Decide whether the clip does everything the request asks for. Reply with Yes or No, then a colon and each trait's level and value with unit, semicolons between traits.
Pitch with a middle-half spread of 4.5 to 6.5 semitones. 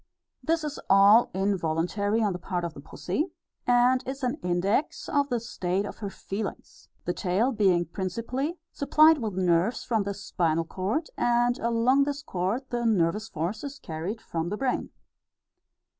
Yes: wide, 5.6 semitones